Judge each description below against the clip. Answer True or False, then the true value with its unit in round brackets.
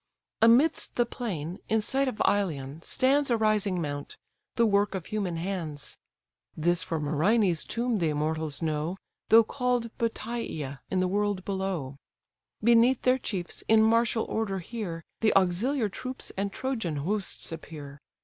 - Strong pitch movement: True (5.9 semitones)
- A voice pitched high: True (200 Hz)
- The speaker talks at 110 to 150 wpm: True (145 wpm)